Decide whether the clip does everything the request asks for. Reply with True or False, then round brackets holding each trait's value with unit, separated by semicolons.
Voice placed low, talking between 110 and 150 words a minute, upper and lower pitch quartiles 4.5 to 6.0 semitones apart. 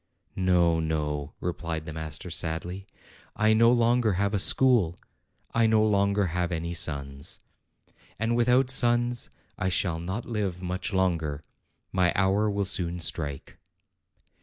True (90 Hz; 135 wpm; 4.8 semitones)